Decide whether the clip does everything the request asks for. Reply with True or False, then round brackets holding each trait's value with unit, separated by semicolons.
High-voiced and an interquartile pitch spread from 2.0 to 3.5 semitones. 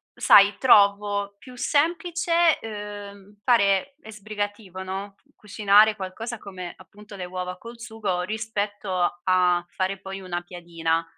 True (200 Hz; 2.7 semitones)